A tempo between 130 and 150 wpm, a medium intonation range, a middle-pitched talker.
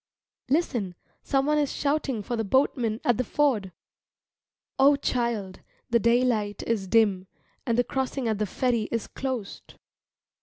No: average, 140 wpm; average, 3.9 semitones; high, 235 Hz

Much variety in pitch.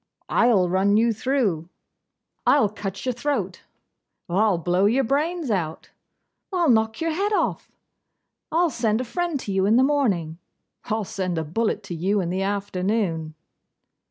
Yes: wide, 5.9 semitones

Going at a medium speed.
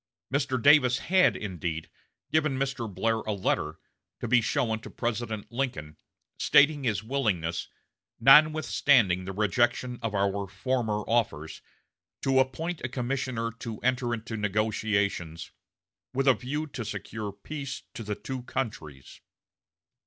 No: slow, 130 wpm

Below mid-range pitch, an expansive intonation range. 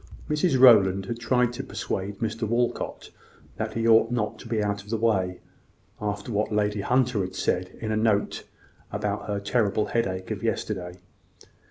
No: low, 105 Hz; narrow, 2.6 semitones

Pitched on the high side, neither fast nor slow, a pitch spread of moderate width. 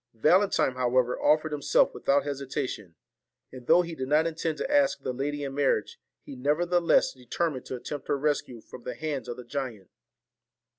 No: medium, 140 Hz; average, 175 wpm; average, 3.5 semitones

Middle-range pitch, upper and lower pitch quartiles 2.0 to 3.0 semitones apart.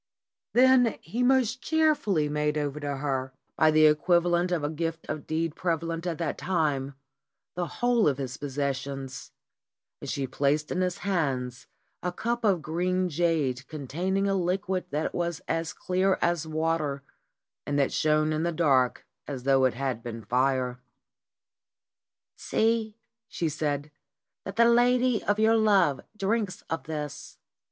No: medium, 160 Hz; average, 4.7 semitones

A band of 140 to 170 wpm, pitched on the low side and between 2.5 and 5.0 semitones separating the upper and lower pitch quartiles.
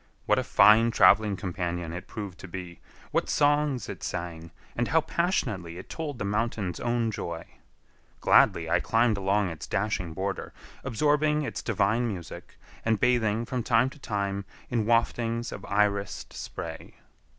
Yes: average, 150 wpm; low, 105 Hz; average, 3.9 semitones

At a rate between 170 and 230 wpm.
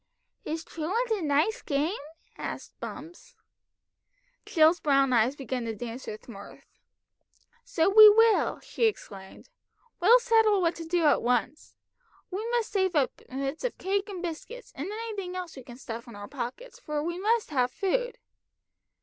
No: average, 160 wpm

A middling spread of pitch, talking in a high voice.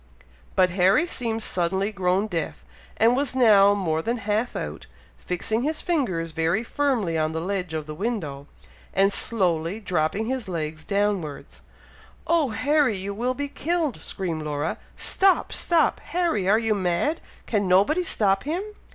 No: wide, 6.1 semitones; high, 200 Hz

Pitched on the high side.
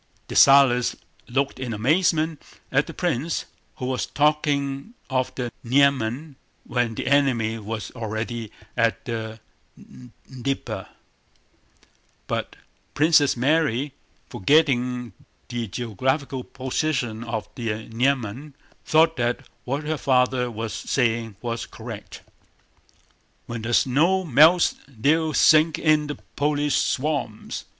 No: low, 130 Hz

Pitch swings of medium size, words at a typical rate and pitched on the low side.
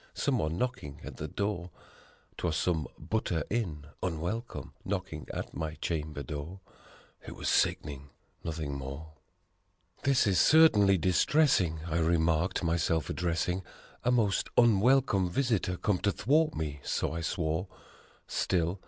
No: average, 4.6 semitones; slow, 130 wpm; very low, 85 Hz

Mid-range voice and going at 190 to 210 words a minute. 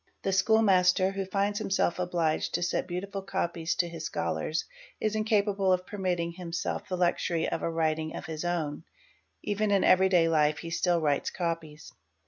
Yes: medium, 175 Hz; average, 195 wpm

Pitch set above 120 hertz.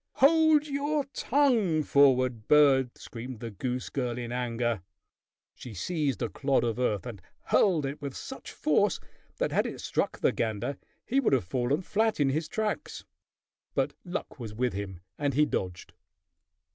Yes: low, 135 Hz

